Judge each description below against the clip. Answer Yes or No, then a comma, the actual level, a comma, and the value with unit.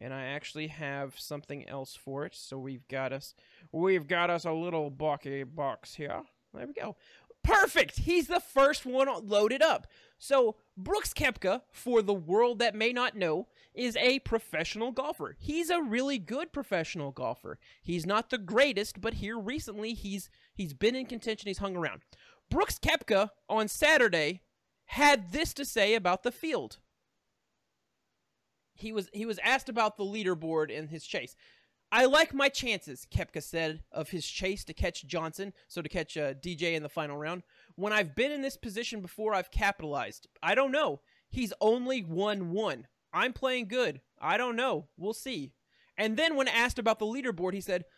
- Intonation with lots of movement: Yes, wide, 7.3 semitones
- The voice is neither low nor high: No, high, 210 Hz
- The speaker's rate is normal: Yes, average, 175 wpm